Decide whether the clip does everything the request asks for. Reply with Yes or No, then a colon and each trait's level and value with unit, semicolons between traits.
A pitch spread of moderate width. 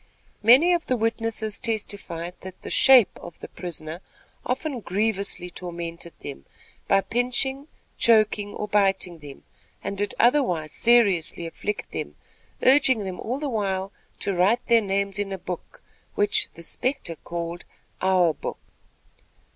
Yes: average, 4.8 semitones